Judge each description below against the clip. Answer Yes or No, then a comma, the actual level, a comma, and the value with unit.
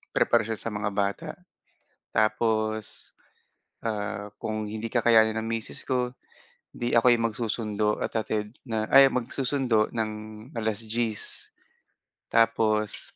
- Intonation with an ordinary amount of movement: No, narrow, 1.4 semitones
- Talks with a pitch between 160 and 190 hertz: No, low, 110 Hz